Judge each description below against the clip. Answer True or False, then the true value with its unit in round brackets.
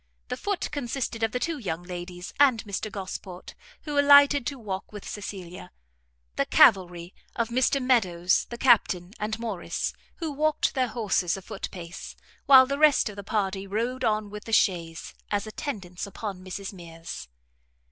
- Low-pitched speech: False (210 Hz)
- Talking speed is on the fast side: False (165 wpm)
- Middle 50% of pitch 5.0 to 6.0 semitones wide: True (5.4 semitones)